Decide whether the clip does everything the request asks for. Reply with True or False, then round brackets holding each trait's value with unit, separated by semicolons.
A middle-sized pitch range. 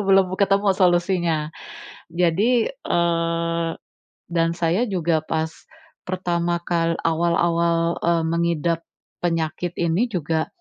False (1.3 semitones)